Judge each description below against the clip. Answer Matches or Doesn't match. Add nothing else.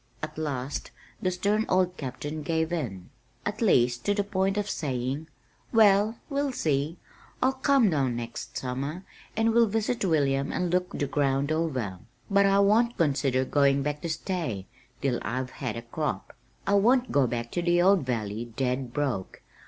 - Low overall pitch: Doesn't match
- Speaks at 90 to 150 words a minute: Doesn't match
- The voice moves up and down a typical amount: Doesn't match